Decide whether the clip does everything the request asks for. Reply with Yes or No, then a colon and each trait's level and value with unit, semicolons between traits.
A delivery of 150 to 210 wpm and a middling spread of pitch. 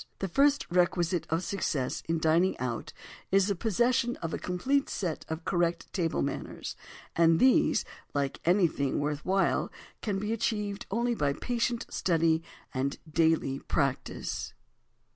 No: slow, 135 wpm; average, 4.6 semitones